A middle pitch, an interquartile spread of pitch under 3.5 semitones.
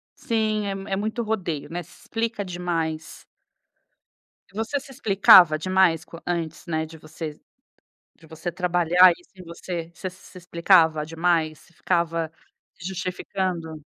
Yes: medium, 175 Hz; average, 2.9 semitones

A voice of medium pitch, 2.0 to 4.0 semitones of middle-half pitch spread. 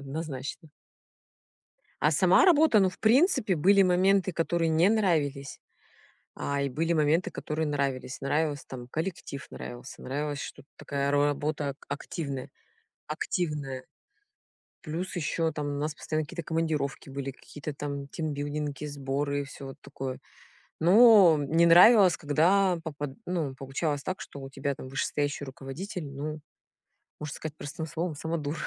Yes: medium, 150 Hz; average, 3.3 semitones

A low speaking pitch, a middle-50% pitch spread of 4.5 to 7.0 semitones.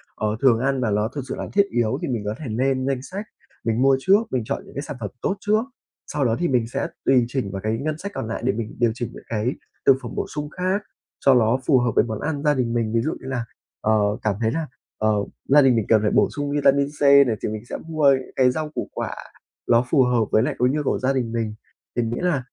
No: low, 130 Hz; average, 3.9 semitones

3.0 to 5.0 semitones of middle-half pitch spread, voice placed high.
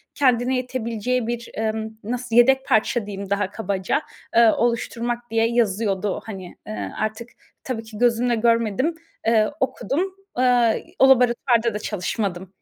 No: narrow, 2.4 semitones; high, 230 Hz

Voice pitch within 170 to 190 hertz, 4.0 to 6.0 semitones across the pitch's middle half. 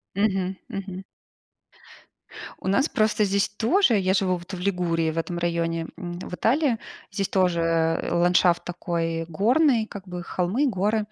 No: medium, 185 Hz; average, 3.3 semitones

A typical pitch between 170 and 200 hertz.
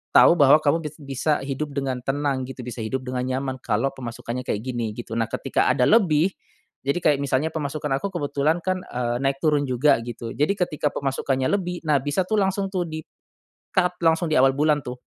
No: medium, 140 Hz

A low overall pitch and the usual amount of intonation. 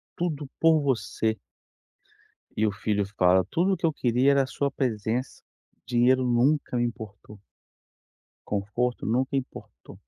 Yes: low, 125 Hz; average, 4.1 semitones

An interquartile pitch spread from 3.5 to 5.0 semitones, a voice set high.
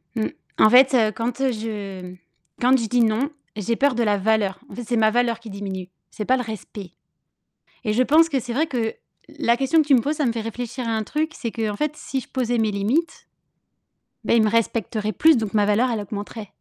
No: average, 3.1 semitones; high, 230 Hz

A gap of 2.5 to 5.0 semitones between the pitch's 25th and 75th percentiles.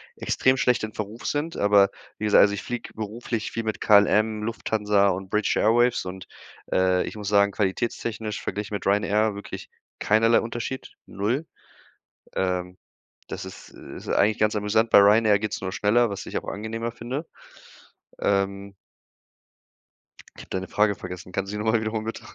No: narrow, 2.0 semitones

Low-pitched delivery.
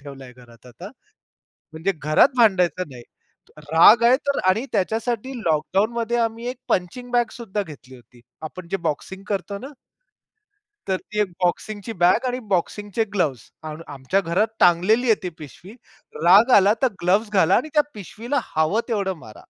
No: high, 195 Hz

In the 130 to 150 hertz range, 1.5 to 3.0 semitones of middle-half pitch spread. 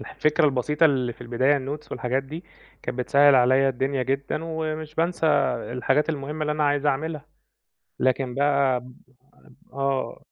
Yes: medium, 140 Hz; narrow, 2.5 semitones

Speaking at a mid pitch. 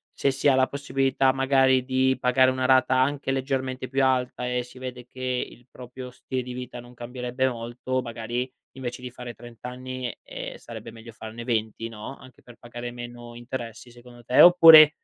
No: low, 125 Hz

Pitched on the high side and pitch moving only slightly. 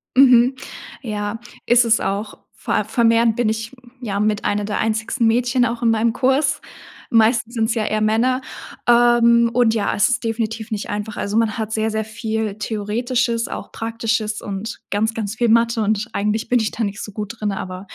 Yes: high, 225 Hz; narrow, 1.6 semitones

